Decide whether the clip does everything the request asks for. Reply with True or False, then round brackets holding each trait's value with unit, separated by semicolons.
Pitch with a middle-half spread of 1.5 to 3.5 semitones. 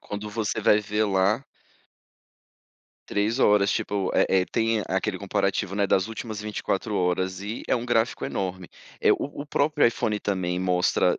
True (2.7 semitones)